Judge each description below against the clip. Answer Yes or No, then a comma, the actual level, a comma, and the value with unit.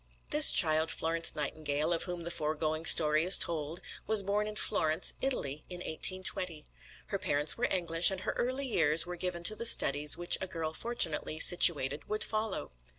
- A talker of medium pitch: Yes, medium, 170 Hz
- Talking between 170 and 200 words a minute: Yes, average, 175 wpm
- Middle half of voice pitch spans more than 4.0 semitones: No, average, 3.7 semitones